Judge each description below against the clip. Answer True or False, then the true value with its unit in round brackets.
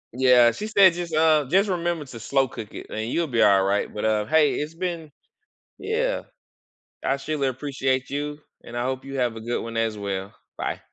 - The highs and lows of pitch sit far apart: True (5.8 semitones)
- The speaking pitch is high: False (135 Hz)